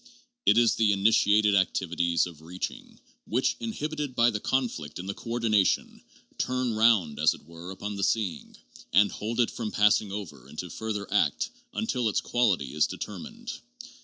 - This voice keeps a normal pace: Yes, average, 160 wpm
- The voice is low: Yes, low, 105 Hz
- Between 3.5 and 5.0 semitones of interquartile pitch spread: Yes, average, 4.5 semitones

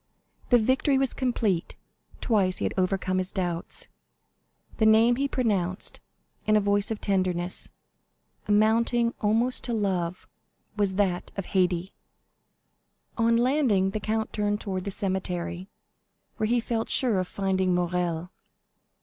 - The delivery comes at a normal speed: No, slow, 130 wpm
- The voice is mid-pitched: No, high, 200 Hz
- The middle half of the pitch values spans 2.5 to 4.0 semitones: Yes, average, 3.6 semitones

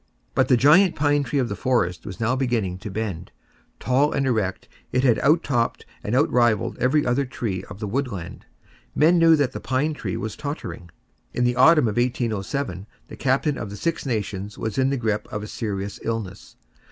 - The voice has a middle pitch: No, low, 120 Hz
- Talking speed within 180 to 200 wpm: Yes, average, 195 wpm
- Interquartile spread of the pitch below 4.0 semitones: No, average, 4.8 semitones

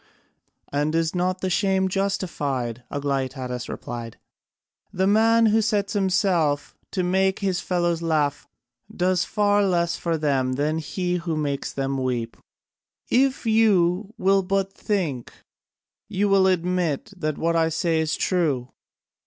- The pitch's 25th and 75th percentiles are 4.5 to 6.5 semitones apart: Yes, average, 4.9 semitones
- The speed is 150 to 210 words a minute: No, slow, 135 wpm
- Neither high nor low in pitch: Yes, medium, 175 Hz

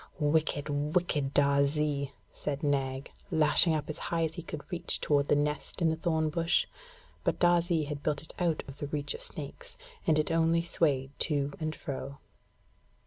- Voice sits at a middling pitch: Yes, medium, 150 Hz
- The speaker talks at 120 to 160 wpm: No, average, 170 wpm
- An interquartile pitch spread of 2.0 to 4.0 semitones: Yes, narrow, 2.4 semitones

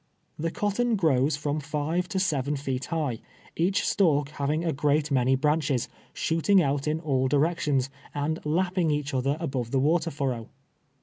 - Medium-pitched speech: Yes, medium, 150 Hz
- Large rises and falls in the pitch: No, average, 3.2 semitones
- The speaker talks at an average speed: Yes, average, 165 wpm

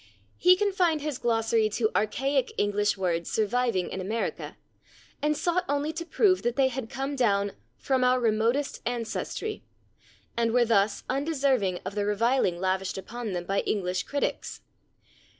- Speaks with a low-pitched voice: No, high, 235 Hz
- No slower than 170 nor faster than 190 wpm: No, average, 150 wpm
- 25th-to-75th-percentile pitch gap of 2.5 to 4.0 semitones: No, average, 5.3 semitones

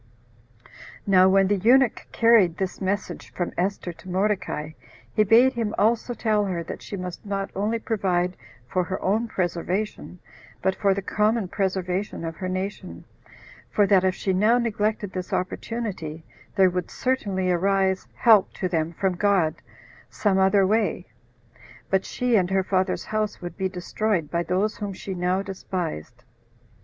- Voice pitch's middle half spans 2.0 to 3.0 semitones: Yes, narrow, 2.5 semitones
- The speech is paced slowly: No, average, 155 wpm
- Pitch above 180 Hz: Yes, high, 190 Hz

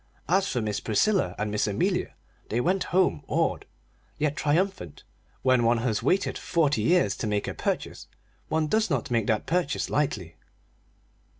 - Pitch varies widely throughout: Yes, wide, 8.6 semitones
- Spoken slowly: No, average, 160 wpm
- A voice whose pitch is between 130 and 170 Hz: Yes, medium, 140 Hz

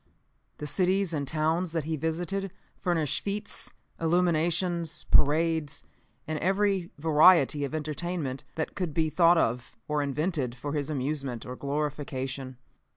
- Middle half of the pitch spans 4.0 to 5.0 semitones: No, average, 3.3 semitones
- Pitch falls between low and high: Yes, medium, 155 Hz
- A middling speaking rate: No, slow, 130 wpm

